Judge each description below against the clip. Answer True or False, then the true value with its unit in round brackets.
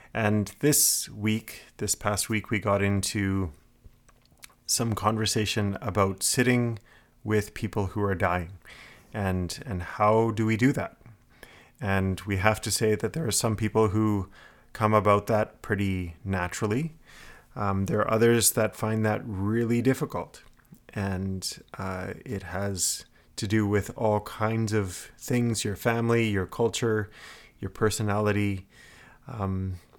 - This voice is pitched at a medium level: False (105 Hz)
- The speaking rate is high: False (135 wpm)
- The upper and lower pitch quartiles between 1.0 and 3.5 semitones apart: True (2.4 semitones)